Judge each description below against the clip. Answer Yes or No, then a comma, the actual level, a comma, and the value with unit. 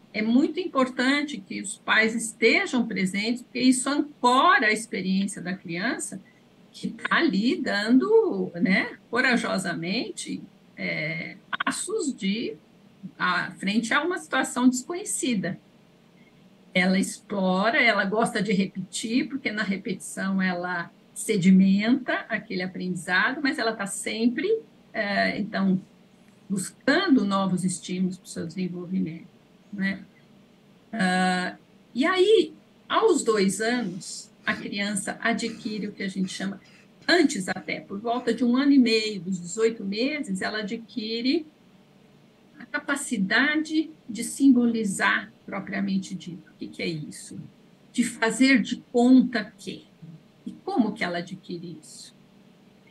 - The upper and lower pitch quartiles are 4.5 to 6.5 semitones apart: No, average, 4.1 semitones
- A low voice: No, high, 215 Hz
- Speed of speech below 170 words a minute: Yes, slow, 120 wpm